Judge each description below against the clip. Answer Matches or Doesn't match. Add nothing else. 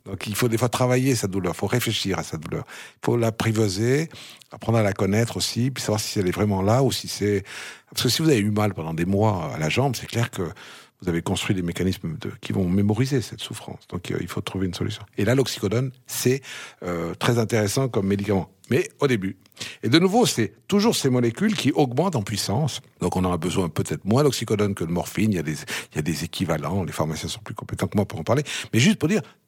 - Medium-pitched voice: Doesn't match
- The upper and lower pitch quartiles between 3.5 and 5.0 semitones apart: Matches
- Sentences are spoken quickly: Matches